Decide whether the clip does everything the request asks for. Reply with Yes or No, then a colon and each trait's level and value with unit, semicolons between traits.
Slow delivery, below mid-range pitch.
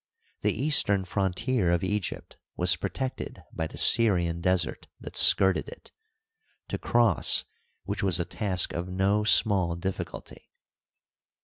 Yes: slow, 125 wpm; very low, 95 Hz